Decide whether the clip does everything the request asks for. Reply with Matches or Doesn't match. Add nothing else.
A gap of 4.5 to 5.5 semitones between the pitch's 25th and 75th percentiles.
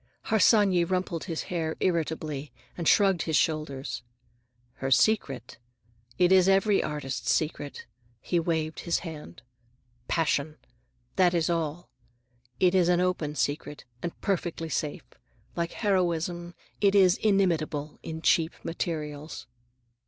Doesn't match